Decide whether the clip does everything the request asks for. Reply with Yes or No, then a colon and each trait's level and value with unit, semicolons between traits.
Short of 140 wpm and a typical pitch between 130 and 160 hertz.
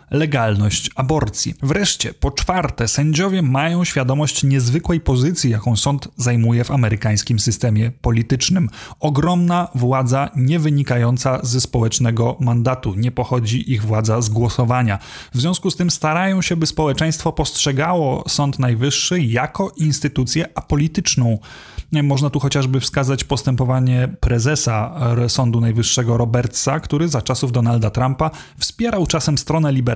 Yes: average, 125 wpm; low, 135 Hz